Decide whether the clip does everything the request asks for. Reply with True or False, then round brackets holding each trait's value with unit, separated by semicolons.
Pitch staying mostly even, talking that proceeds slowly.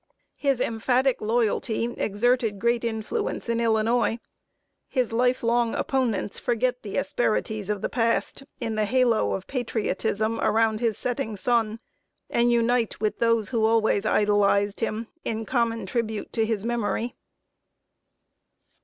True (1.9 semitones; 130 wpm)